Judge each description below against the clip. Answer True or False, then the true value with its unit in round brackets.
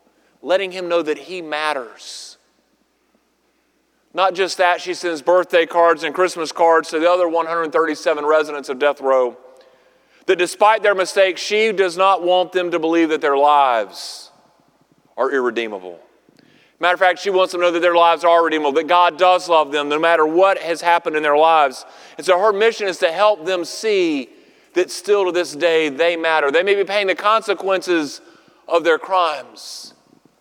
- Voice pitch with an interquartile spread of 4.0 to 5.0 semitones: False (2.8 semitones)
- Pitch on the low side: False (175 Hz)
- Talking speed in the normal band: True (180 wpm)